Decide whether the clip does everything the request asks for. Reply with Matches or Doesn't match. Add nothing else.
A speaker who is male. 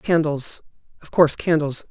Matches